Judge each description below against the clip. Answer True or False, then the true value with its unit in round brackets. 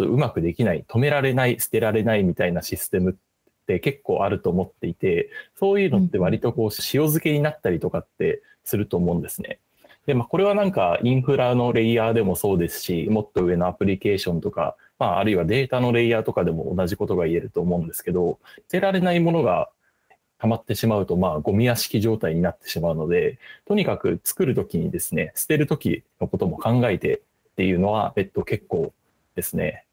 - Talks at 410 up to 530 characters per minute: True (440 characters per minute)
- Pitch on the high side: False (120 Hz)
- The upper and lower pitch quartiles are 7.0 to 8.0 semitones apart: True (7.7 semitones)